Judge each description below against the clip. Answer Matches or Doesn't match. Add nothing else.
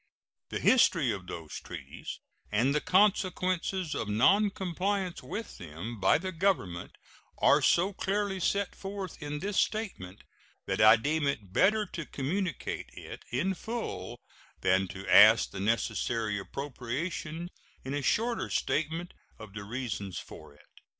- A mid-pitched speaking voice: Matches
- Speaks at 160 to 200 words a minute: Doesn't match